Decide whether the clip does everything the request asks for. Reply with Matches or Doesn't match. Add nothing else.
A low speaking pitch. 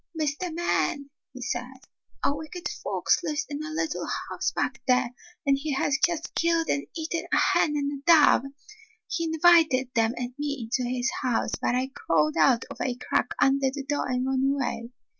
Doesn't match